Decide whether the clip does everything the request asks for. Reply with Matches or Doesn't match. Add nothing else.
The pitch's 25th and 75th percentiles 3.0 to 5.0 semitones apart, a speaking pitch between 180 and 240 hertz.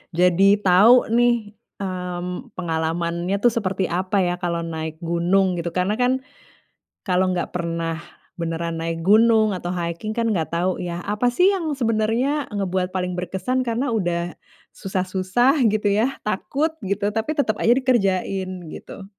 Matches